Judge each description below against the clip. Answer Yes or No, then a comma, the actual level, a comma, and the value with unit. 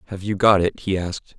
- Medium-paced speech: No, fast, 260 wpm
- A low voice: Yes, very low, 95 Hz